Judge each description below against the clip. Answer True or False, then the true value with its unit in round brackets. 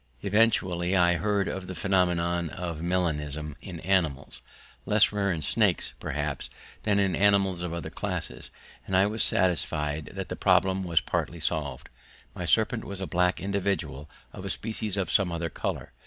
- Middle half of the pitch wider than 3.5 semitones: False (3.0 semitones)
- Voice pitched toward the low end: True (90 Hz)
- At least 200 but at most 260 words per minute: False (165 wpm)